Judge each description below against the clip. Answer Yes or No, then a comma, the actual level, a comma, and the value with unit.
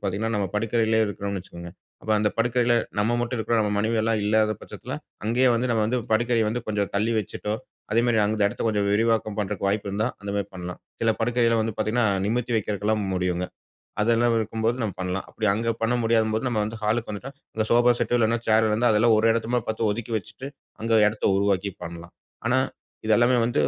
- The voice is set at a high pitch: No, low, 110 Hz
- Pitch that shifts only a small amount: Yes, narrow, 2.1 semitones